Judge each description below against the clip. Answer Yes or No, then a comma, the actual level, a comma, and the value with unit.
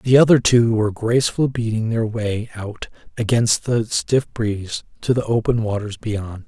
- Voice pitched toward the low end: Yes, low, 115 Hz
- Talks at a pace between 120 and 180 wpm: Yes, average, 165 wpm